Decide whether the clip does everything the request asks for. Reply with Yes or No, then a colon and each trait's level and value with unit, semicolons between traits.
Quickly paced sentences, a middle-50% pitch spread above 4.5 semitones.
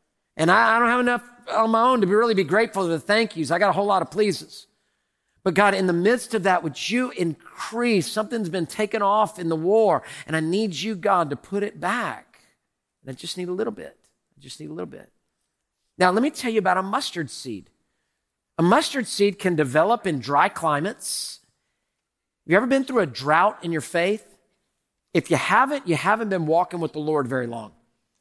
Yes: fast, 215 wpm; average, 4.9 semitones